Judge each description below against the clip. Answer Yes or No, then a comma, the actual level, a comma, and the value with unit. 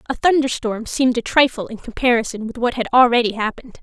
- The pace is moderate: Yes, average, 190 wpm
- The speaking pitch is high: Yes, high, 240 Hz